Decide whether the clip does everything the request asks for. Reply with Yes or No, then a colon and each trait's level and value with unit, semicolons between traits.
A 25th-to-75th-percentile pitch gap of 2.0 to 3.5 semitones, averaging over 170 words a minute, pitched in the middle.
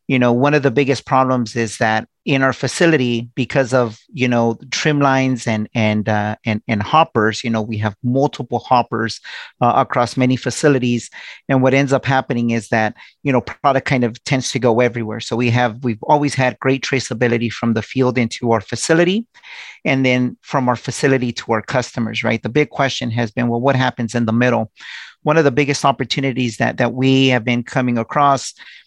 No: narrow, 2.6 semitones; average, 200 wpm; low, 125 Hz